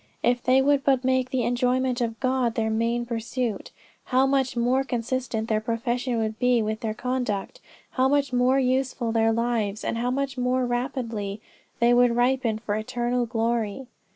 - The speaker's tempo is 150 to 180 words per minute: Yes, average, 170 wpm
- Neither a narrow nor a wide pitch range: No, narrow, 2.1 semitones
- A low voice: No, high, 245 Hz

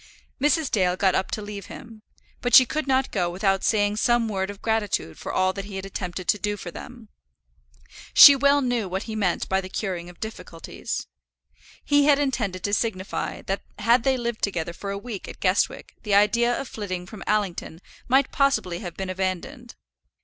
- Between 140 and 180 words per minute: No, average, 195 wpm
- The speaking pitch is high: Yes, high, 205 Hz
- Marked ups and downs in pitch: No, average, 4.2 semitones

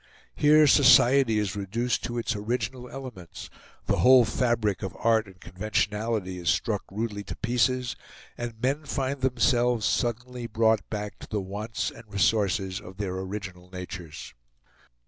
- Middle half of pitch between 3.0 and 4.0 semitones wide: Yes, average, 3.6 semitones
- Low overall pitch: Yes, low, 110 Hz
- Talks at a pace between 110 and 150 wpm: Yes, average, 145 wpm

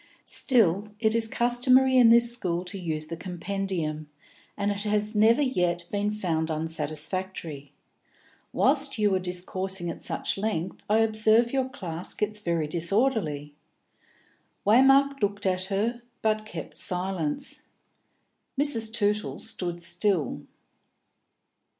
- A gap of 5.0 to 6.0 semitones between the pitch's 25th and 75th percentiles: No, average, 4.6 semitones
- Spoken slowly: Yes, slow, 120 wpm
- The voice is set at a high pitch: Yes, high, 200 Hz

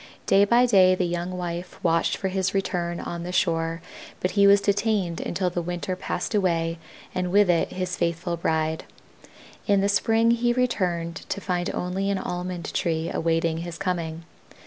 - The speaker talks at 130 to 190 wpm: Yes, average, 170 wpm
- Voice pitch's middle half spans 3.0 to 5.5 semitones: No, narrow, 2.6 semitones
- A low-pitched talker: No, medium, 180 Hz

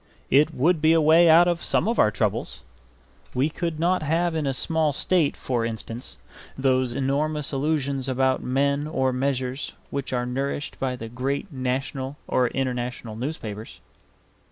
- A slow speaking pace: No, average, 155 wpm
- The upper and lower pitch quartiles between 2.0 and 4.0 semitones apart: Yes, average, 3.4 semitones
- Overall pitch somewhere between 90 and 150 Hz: Yes, low, 135 Hz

